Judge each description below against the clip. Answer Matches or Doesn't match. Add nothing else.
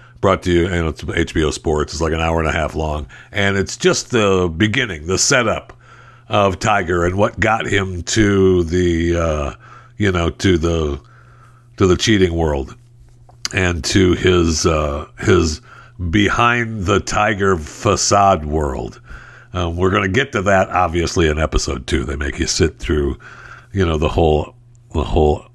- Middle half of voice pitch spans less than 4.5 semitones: Doesn't match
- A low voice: Matches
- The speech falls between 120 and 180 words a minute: Matches